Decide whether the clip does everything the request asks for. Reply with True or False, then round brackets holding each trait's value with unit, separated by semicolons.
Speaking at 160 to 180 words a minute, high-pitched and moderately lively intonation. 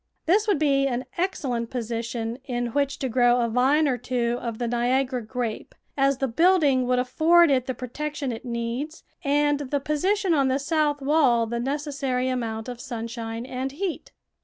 True (175 wpm; 260 Hz; 3.4 semitones)